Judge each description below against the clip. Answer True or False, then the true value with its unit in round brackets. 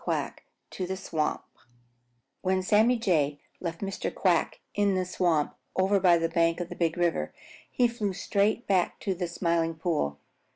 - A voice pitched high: False (180 Hz)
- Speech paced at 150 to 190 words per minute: True (165 wpm)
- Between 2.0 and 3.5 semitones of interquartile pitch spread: True (2.9 semitones)